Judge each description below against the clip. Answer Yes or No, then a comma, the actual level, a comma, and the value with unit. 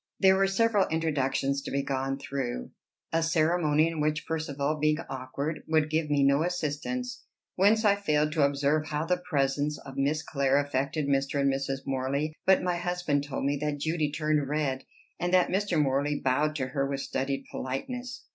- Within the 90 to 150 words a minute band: No, average, 180 wpm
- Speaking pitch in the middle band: Yes, medium, 150 Hz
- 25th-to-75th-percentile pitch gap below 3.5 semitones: Yes, average, 2.9 semitones